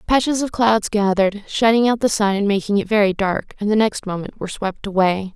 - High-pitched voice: Yes, high, 210 Hz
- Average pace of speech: No, fast, 225 wpm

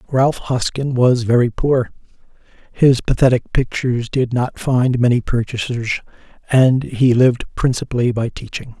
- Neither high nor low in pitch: No, low, 125 Hz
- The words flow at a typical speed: No, slow, 130 wpm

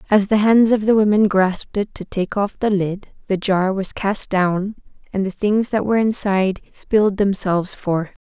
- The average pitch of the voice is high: Yes, high, 200 Hz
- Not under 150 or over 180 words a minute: No, average, 195 wpm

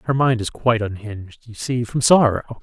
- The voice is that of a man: Yes, male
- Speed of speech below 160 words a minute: No, fast, 205 wpm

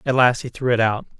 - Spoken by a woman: No, male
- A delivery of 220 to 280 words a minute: No, fast, 300 wpm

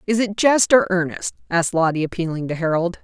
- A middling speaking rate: Yes, average, 195 wpm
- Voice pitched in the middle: Yes, medium, 180 Hz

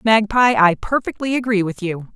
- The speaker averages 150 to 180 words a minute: Yes, average, 165 wpm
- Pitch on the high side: Yes, high, 210 Hz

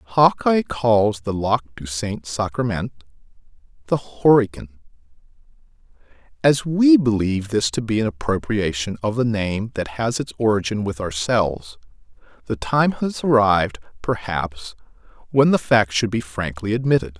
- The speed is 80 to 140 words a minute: Yes, slow, 135 wpm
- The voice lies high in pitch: No, low, 110 Hz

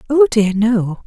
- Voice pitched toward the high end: Yes, high, 225 Hz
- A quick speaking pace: No, average, 170 wpm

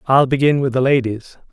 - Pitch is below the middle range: Yes, low, 130 Hz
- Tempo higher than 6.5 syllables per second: No, 5.4 syllables/s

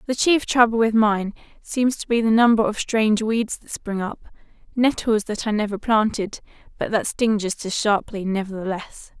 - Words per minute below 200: Yes, average, 175 wpm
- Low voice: No, high, 220 Hz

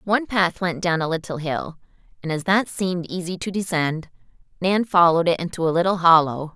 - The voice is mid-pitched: Yes, medium, 175 Hz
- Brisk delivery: No, average, 190 wpm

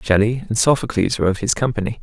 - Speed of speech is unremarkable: No, fast, 210 wpm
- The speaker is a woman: No, male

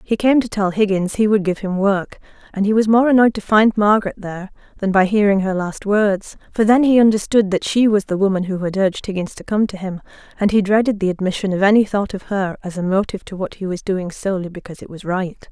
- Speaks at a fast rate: Yes, fast, 250 wpm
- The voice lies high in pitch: Yes, high, 200 Hz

